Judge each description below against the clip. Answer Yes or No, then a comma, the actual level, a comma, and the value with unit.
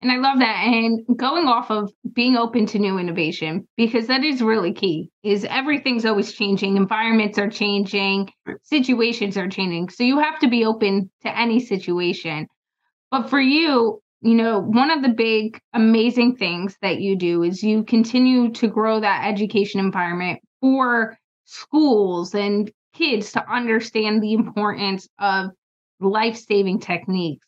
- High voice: Yes, high, 220 Hz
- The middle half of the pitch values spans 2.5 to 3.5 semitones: Yes, average, 3.2 semitones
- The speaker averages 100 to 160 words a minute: Yes, average, 155 wpm